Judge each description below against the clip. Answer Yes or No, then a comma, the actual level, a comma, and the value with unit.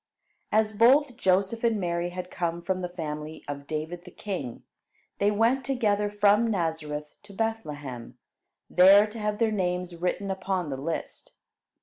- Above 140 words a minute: Yes, average, 150 wpm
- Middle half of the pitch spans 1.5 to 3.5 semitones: No, average, 4.2 semitones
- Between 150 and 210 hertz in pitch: Yes, medium, 185 Hz